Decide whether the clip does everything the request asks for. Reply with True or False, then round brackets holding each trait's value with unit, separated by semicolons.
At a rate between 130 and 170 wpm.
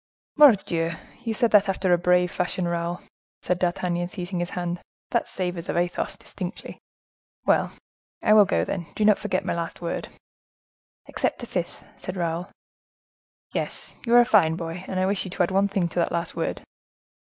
False (185 wpm)